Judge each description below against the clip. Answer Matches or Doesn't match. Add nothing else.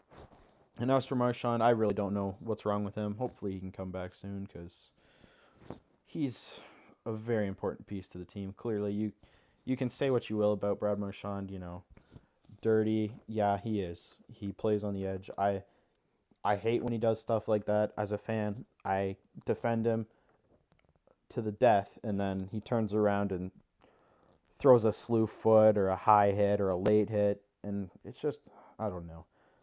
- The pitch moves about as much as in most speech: Doesn't match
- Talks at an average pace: Matches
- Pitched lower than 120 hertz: Matches